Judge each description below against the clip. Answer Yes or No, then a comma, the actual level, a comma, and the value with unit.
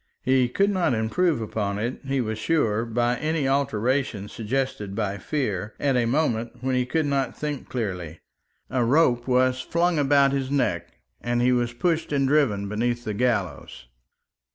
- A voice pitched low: Yes, low, 125 Hz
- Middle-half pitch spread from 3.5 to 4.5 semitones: Yes, average, 3.9 semitones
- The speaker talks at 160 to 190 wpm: Yes, average, 165 wpm